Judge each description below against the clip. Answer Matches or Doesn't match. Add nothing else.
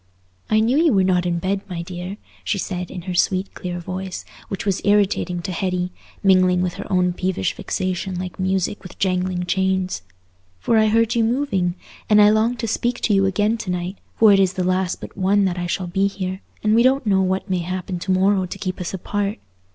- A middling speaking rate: Doesn't match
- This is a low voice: Doesn't match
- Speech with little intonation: Matches